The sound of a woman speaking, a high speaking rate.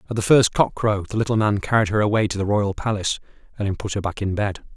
No: male; fast, 265 wpm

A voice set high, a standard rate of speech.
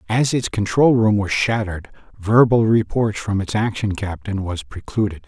No: low, 105 Hz; average, 160 wpm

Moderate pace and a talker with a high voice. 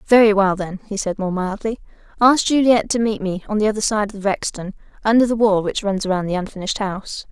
No: fast, 220 wpm; high, 205 Hz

